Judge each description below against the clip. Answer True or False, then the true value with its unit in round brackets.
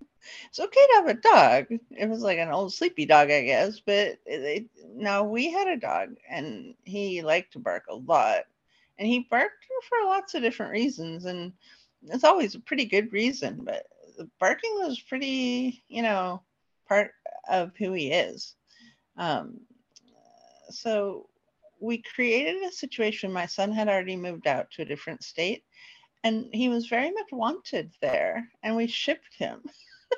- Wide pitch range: True (7.7 semitones)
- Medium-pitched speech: False (235 Hz)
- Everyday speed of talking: True (160 wpm)